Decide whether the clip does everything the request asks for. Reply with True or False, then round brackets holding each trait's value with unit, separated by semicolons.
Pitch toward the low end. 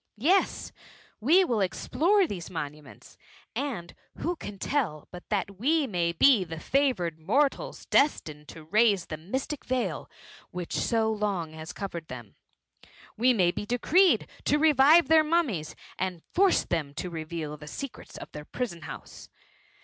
False (205 Hz)